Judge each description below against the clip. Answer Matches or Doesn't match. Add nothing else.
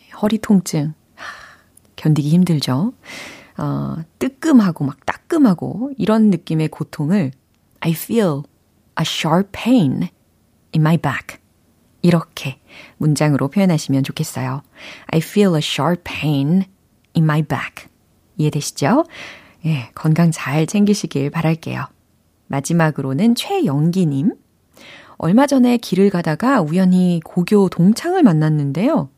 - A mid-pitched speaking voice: Matches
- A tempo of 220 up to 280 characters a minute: Doesn't match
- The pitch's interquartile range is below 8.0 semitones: Matches